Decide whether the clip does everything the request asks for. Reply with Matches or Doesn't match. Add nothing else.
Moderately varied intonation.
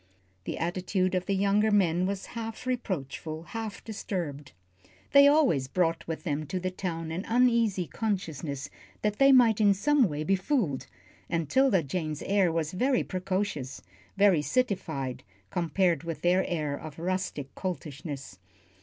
Matches